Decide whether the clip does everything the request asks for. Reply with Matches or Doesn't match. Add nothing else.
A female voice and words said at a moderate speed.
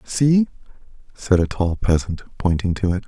Doesn't match